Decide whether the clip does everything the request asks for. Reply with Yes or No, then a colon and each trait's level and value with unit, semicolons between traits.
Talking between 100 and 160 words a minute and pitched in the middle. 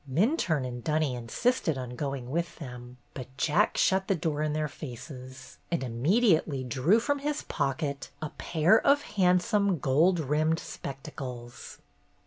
Yes: average, 140 wpm; medium, 150 Hz